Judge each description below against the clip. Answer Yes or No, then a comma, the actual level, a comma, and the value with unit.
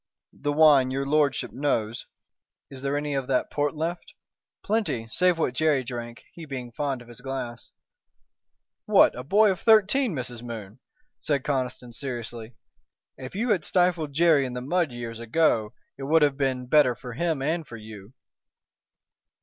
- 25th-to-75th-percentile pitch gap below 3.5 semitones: No, average, 4.5 semitones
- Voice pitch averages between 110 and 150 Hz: Yes, low, 135 Hz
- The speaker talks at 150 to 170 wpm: Yes, average, 165 wpm